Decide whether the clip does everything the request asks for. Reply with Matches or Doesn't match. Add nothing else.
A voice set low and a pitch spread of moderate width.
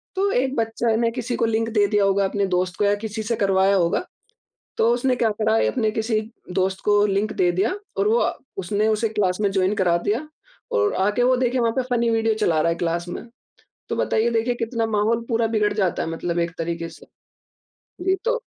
Doesn't match